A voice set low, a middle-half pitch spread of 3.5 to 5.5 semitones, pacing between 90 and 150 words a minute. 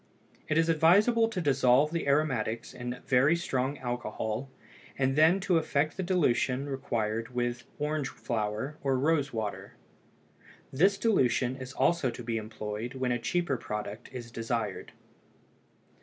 Yes: low, 130 Hz; average, 4.7 semitones; average, 140 wpm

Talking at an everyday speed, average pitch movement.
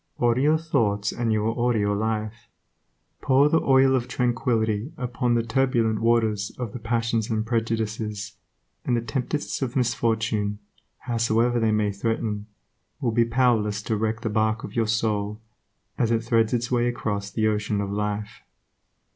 No: average, 165 wpm; narrow, 2.0 semitones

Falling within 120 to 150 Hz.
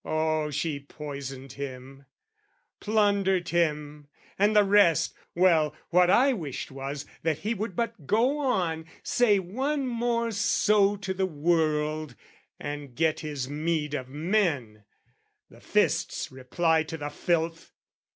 No: medium, 160 Hz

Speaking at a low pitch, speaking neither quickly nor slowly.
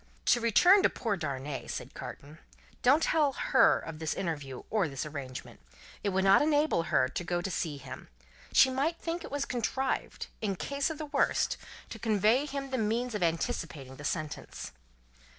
No: high, 210 Hz; average, 185 wpm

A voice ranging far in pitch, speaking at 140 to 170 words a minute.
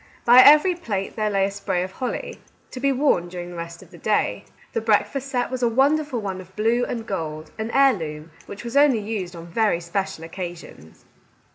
No: wide, 6.2 semitones; fast, 205 wpm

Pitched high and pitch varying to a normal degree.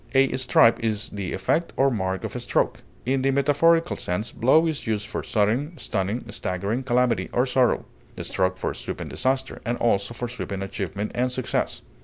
No: low, 120 Hz; average, 4.6 semitones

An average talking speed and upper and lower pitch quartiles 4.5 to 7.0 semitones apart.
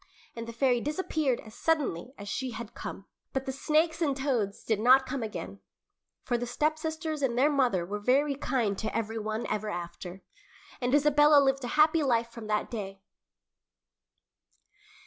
Yes: average, 165 wpm; average, 5.0 semitones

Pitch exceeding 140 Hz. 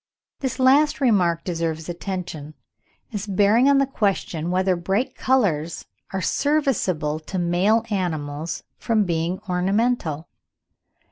Yes: medium, 185 Hz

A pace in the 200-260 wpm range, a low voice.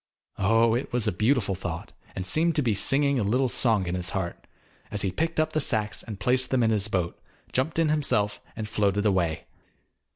Yes: fast, 205 wpm; low, 110 Hz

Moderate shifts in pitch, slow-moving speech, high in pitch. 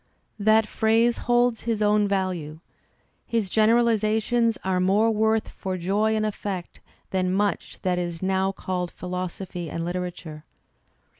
Yes: average, 3.2 semitones; slow, 130 wpm; high, 200 Hz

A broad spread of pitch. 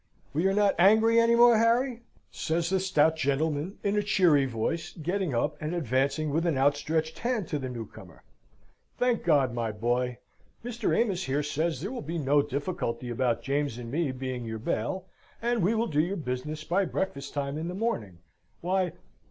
Yes: wide, 6.1 semitones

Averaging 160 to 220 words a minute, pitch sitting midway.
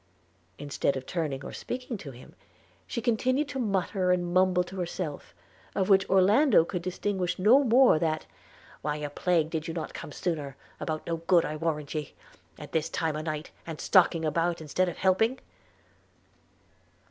Yes: average, 170 wpm; medium, 175 Hz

